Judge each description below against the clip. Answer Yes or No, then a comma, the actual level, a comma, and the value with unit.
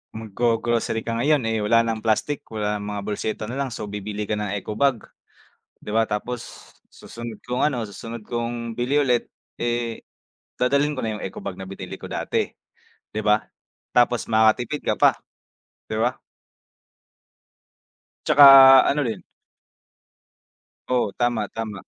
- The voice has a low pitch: Yes, low, 115 Hz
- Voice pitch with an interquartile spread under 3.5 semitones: Yes, narrow, 2.5 semitones